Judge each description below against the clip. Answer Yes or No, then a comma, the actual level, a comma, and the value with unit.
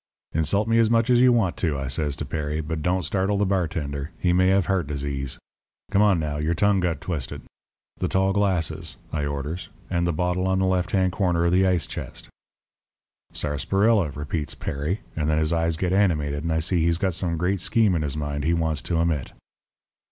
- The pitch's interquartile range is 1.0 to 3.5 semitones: No, average, 3.9 semitones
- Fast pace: Yes, fast, 210 wpm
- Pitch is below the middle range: Yes, very low, 85 Hz